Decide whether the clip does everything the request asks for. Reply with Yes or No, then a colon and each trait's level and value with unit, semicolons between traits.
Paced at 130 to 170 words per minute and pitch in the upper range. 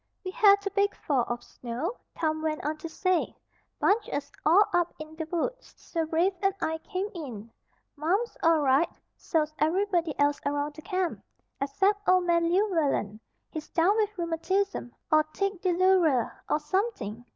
Yes: average, 160 wpm; very high, 330 Hz